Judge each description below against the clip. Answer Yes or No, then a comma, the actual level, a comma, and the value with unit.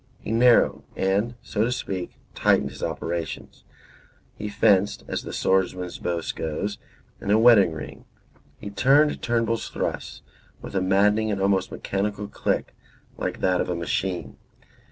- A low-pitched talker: Yes, low, 100 Hz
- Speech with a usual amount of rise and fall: Yes, average, 3.1 semitones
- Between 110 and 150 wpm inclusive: Yes, average, 145 wpm